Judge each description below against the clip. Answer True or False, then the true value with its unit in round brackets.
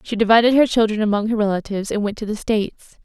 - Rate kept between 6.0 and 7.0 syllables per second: True (6.9 syllables/s)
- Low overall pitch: False (215 Hz)